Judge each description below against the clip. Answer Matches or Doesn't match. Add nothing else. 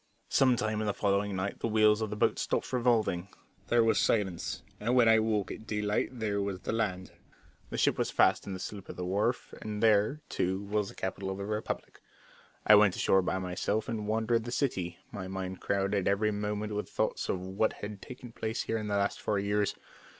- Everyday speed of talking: Doesn't match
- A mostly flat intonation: Matches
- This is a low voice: Matches